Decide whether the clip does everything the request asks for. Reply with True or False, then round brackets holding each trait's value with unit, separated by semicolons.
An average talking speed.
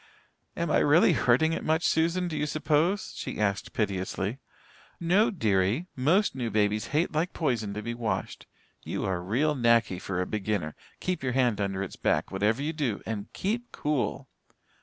True (175 wpm)